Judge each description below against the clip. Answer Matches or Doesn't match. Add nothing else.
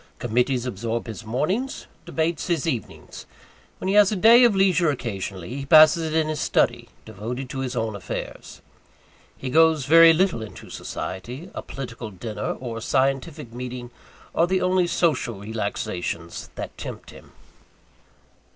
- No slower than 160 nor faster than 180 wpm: Doesn't match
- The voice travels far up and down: Matches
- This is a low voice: Matches